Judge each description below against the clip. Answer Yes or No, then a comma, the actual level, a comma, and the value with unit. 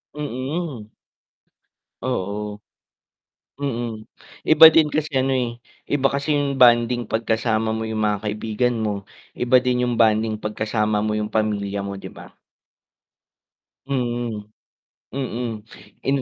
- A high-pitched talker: No, low, 120 Hz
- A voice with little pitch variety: No, average, 3.4 semitones